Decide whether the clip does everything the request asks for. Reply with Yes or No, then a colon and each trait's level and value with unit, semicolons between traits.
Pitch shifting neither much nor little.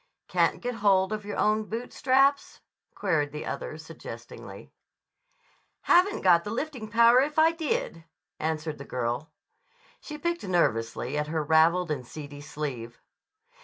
No: wide, 8.6 semitones